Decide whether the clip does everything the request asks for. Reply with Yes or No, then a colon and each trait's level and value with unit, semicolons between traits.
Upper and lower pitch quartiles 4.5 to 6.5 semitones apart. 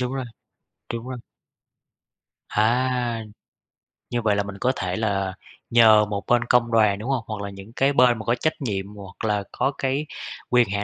No: average, 3.4 semitones